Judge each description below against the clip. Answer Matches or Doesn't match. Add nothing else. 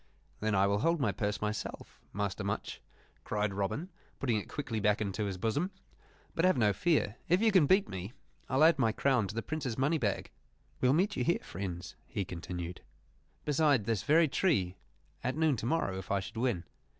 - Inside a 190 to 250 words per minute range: Matches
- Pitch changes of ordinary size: Doesn't match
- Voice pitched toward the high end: Doesn't match